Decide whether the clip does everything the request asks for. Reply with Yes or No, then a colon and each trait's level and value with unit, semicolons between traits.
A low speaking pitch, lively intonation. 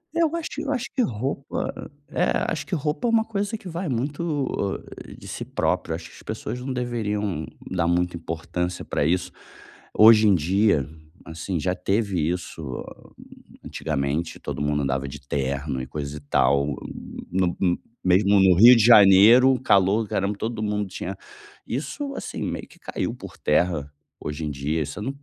Yes: very low, 95 Hz; wide, 7.8 semitones